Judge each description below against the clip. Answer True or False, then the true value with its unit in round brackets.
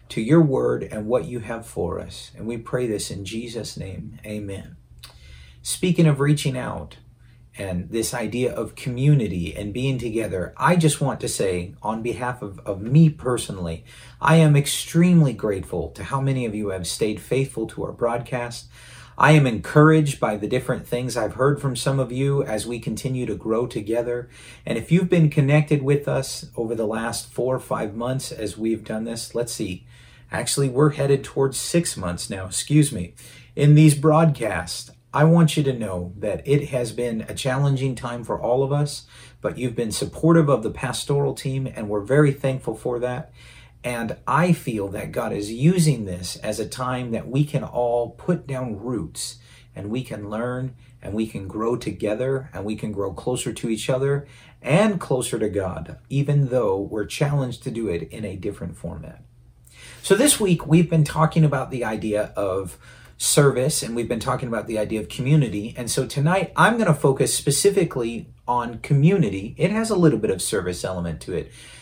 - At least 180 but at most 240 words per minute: True (190 wpm)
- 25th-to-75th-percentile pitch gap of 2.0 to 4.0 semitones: False (4.5 semitones)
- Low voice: True (125 Hz)